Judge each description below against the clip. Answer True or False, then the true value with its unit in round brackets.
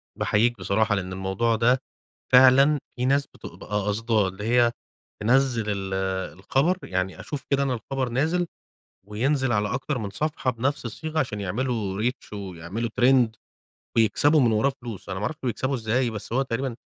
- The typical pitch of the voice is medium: False (120 Hz)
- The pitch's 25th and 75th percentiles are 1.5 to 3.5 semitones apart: False (4.2 semitones)